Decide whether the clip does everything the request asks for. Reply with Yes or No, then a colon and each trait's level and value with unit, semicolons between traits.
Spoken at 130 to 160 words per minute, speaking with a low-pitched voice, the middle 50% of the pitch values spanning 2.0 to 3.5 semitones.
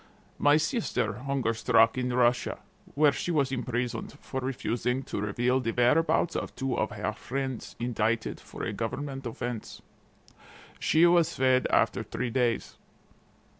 Yes: average, 140 wpm; low, 125 Hz; narrow, 2.6 semitones